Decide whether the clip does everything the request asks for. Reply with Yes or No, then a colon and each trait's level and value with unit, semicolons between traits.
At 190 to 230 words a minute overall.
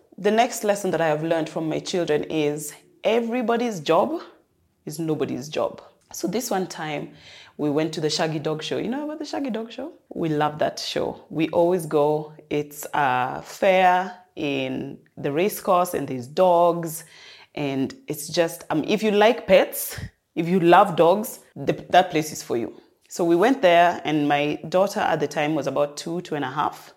Yes: average, 195 wpm